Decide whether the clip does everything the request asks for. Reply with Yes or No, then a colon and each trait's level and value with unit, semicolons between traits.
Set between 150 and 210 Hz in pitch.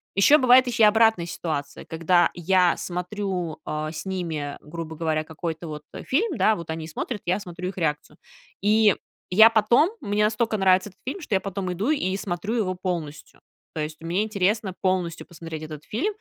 Yes: medium, 185 Hz